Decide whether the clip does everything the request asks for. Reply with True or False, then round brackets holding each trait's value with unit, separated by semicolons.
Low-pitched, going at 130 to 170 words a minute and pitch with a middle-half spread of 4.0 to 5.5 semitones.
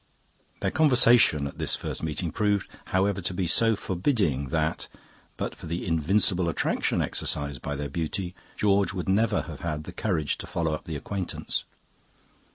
True (90 Hz; 165 wpm; 4.6 semitones)